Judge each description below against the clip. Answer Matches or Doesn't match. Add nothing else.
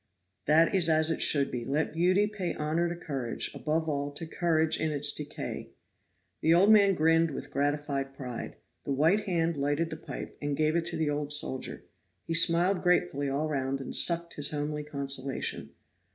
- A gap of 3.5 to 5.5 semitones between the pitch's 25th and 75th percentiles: Doesn't match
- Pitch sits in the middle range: Matches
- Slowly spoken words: Doesn't match